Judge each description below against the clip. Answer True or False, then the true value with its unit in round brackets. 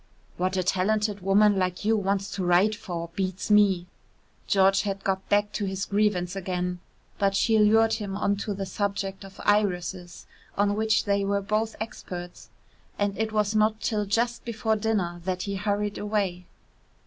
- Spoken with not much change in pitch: True (1.9 semitones)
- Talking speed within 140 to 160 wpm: False (170 wpm)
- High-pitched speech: True (200 Hz)